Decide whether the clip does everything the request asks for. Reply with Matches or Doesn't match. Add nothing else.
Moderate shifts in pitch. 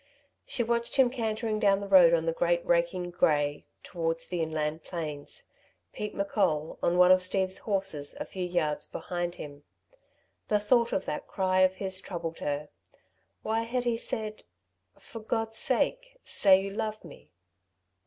Matches